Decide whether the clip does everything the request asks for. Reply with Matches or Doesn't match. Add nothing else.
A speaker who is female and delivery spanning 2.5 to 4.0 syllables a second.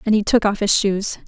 Doesn't match